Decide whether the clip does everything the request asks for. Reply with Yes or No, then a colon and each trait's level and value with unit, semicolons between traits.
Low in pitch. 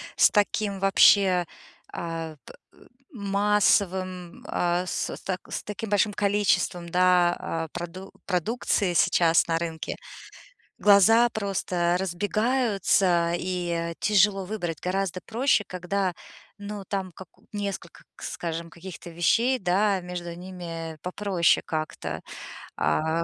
No: medium, 185 Hz